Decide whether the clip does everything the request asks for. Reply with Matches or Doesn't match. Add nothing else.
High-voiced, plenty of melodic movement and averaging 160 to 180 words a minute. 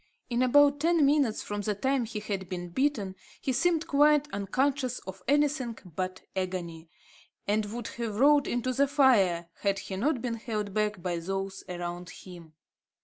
Matches